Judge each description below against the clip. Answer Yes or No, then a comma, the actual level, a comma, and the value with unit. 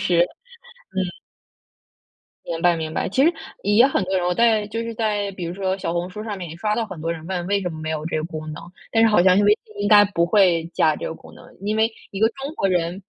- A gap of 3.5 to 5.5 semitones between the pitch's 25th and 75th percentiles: Yes, average, 3.9 semitones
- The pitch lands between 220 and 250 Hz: No, high, 190 Hz